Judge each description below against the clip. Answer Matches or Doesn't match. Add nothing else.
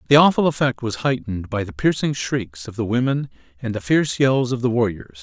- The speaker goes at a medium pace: Doesn't match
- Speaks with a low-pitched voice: Matches